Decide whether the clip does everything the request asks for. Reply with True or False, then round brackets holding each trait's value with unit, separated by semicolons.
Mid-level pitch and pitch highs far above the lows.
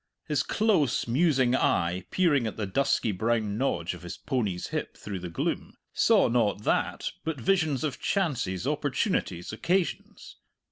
False (120 Hz; 7.3 semitones)